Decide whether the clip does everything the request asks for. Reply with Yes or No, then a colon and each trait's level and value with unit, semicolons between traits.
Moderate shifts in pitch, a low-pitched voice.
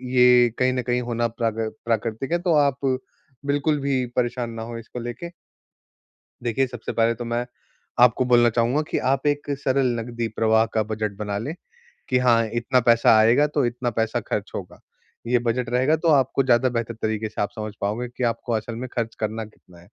No: narrow, 2.2 semitones; low, 120 Hz